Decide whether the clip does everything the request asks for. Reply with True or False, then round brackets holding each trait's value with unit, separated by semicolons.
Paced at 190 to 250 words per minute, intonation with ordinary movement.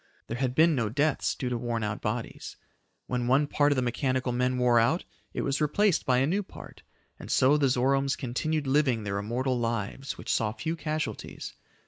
True (195 wpm; 3.4 semitones)